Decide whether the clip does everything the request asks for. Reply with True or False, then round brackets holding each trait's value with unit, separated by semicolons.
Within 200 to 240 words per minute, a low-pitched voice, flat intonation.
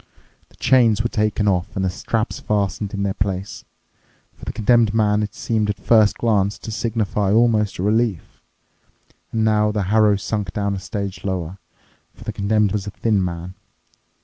False (175 wpm; 105 Hz; 1.9 semitones)